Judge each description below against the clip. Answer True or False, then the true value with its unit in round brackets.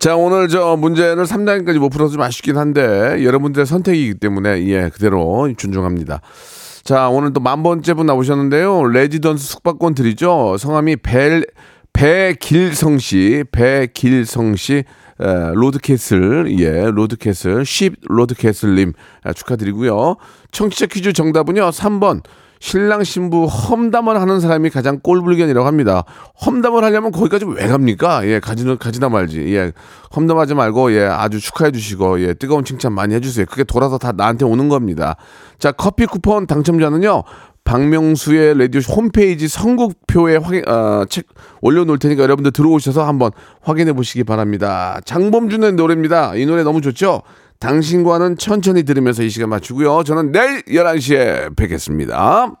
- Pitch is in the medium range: True (145 Hz)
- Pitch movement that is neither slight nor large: False (6.8 semitones)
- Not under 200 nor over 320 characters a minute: False (340 characters per minute)